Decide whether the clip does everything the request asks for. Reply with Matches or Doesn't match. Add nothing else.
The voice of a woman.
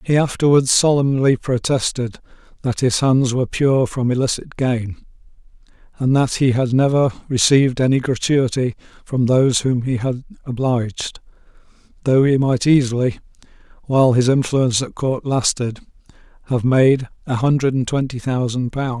Doesn't match